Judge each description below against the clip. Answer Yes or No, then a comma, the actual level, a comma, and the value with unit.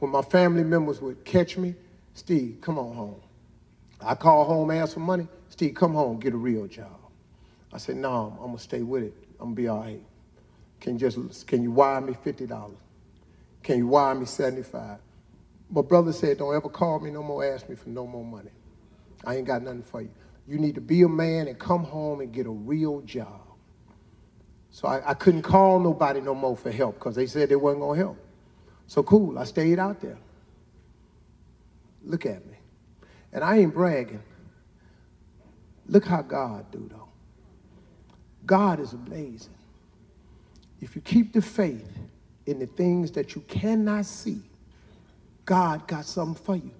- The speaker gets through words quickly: No, average, 185 wpm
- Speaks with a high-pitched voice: No, medium, 145 Hz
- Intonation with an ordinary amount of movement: No, wide, 6.2 semitones